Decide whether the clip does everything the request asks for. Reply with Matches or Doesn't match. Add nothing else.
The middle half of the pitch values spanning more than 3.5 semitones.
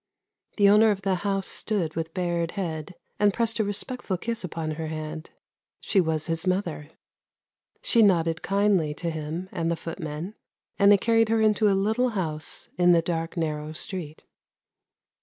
Matches